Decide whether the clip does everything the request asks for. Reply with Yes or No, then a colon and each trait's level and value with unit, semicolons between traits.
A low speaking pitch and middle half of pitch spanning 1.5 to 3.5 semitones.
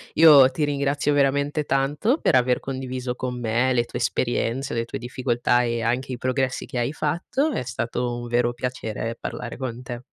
Yes: low, 125 Hz; narrow, 2.4 semitones